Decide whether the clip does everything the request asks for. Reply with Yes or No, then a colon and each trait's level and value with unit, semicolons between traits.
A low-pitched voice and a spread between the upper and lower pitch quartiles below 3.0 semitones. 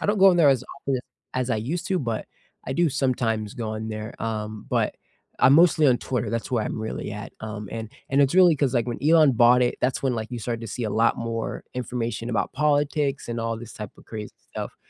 No: low, 120 Hz; average, 3.8 semitones